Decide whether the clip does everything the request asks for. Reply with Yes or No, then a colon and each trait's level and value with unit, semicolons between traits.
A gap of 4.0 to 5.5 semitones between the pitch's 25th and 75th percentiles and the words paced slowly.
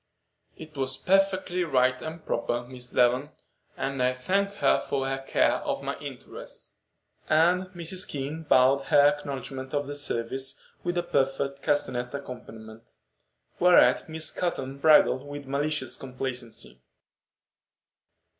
No: average, 3.6 semitones; slow, 125 wpm